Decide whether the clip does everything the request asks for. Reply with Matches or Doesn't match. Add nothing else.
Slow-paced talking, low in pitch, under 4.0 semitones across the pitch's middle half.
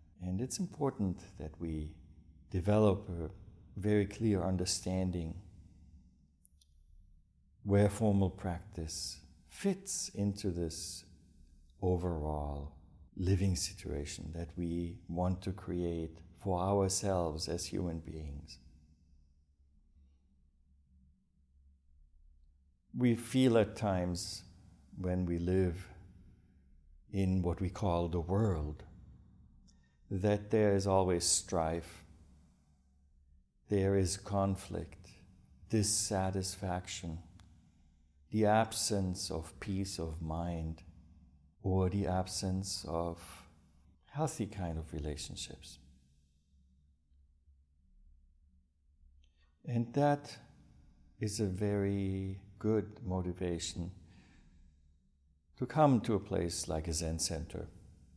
Doesn't match